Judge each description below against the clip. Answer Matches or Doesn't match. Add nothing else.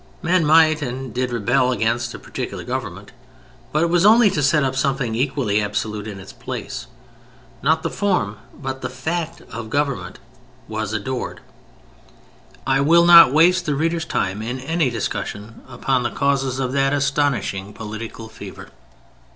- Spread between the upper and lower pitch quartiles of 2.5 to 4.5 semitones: Doesn't match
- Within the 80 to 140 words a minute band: Doesn't match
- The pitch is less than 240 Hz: Matches